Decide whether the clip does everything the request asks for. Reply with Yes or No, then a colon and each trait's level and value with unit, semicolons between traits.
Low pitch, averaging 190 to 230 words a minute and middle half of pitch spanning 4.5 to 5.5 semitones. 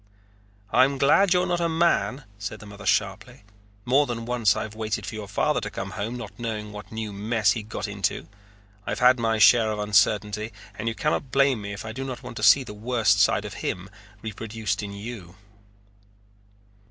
No: low, 110 Hz; average, 200 wpm; average, 3.0 semitones